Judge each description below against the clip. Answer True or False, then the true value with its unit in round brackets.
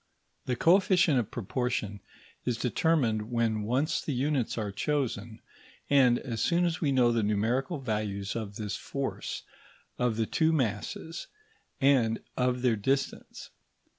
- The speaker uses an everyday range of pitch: True (4.3 semitones)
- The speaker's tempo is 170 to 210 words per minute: False (135 wpm)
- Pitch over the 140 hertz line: False (125 Hz)